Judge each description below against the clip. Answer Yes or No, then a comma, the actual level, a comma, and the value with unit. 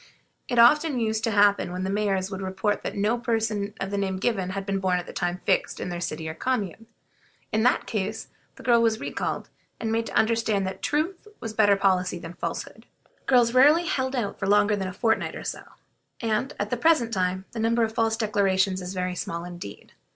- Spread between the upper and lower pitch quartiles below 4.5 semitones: Yes, average, 3.4 semitones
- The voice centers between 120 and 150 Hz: No, high, 205 Hz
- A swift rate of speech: Yes, fast, 210 wpm